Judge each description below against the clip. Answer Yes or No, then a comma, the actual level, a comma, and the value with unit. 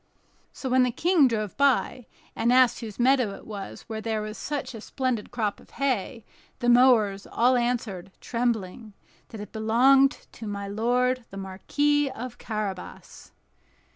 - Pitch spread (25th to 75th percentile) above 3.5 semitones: No, average, 3.2 semitones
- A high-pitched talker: Yes, high, 235 Hz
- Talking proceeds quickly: No, average, 155 wpm